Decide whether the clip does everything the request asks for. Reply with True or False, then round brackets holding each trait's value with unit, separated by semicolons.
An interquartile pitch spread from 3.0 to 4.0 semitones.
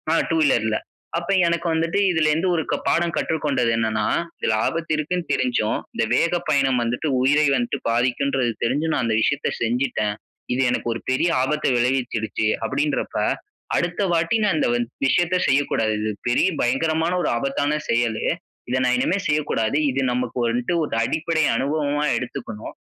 False (5.0 semitones)